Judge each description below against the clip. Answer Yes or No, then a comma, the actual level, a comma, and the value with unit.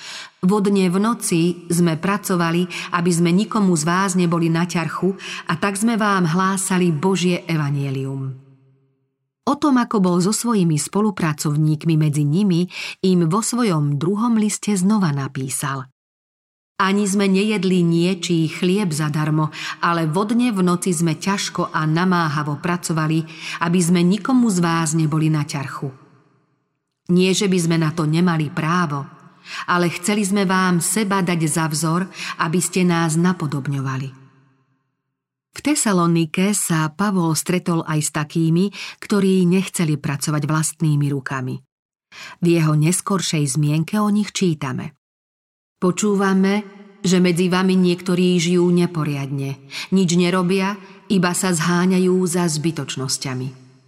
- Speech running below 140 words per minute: Yes, average, 130 wpm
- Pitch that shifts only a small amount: No, average, 3.7 semitones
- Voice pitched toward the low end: No, medium, 175 Hz